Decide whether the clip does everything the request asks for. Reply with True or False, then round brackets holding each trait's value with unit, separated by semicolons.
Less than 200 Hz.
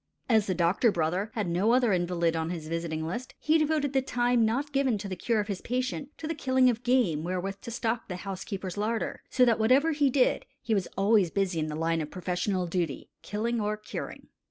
False (210 Hz)